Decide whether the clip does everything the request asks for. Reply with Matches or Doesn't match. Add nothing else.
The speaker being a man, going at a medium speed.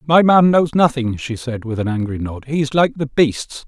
Doesn't match